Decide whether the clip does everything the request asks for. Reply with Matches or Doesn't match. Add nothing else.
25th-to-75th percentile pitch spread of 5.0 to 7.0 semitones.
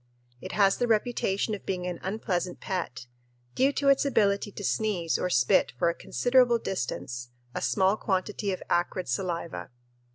Doesn't match